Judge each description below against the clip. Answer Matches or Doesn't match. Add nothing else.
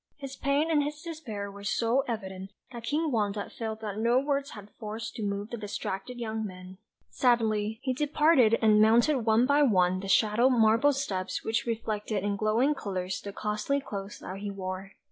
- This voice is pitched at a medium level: Doesn't match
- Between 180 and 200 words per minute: Matches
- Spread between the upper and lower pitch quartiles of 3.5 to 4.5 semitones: Matches